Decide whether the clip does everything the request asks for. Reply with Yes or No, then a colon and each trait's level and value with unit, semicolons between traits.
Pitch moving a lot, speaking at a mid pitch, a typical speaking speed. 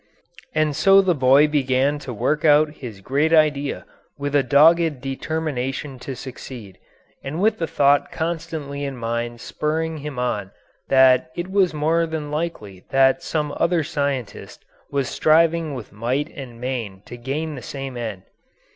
No: average, 3.7 semitones; medium, 145 Hz; average, 155 wpm